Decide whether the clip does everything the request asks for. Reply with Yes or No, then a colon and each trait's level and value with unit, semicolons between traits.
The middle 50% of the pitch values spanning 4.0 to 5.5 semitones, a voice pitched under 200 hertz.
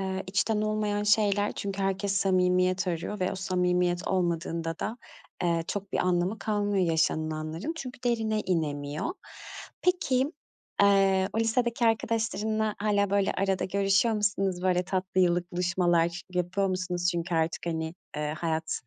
No: average, 2.9 semitones; high, 190 Hz